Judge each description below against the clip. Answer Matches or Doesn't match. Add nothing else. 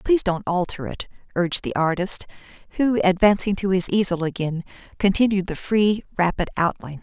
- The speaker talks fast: Doesn't match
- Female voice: Matches